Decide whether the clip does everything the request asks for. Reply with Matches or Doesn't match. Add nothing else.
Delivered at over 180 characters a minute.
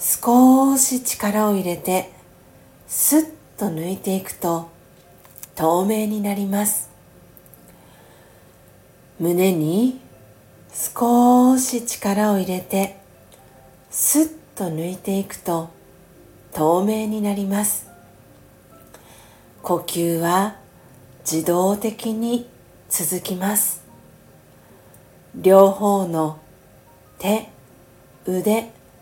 Doesn't match